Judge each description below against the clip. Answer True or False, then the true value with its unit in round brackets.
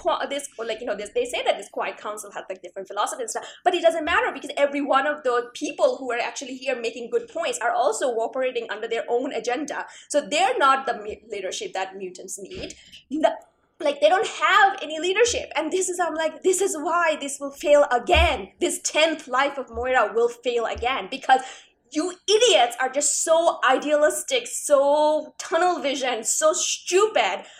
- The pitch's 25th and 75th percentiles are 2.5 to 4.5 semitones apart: False (4.9 semitones)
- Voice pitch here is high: True (295 Hz)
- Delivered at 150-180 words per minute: False (190 wpm)